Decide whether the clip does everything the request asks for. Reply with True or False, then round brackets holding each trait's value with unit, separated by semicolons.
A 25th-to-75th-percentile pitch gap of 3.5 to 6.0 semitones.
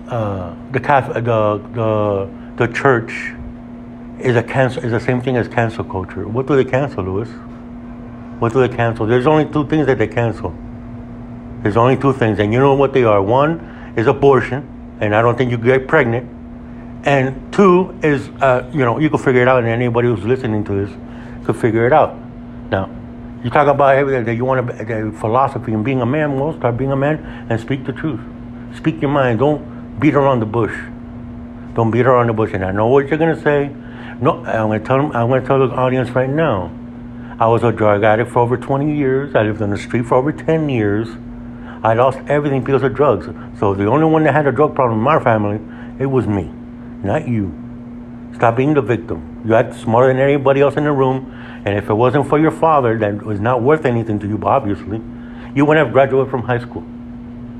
False (2.5 semitones)